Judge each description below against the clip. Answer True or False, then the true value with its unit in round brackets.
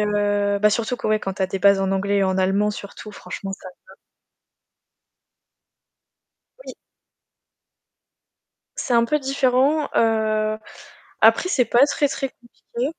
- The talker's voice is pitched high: True (215 Hz)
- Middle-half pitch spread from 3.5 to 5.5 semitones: True (3.8 semitones)